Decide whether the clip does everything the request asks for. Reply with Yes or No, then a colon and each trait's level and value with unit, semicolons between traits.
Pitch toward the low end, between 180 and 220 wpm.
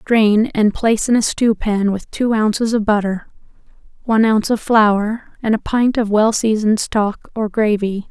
No: high, 215 Hz; average, 185 wpm